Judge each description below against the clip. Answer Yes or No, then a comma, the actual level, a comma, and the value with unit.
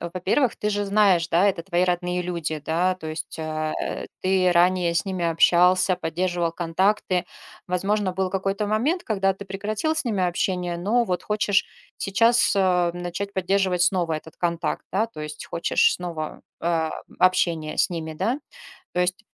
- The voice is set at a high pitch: No, medium, 180 Hz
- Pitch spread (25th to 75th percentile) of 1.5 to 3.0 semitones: Yes, narrow, 2.5 semitones